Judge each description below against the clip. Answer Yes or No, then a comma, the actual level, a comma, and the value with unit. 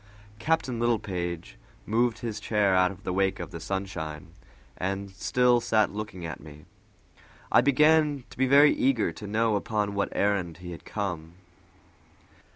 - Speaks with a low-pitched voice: Yes, low, 100 Hz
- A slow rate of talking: No, average, 155 wpm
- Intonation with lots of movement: No, average, 4.6 semitones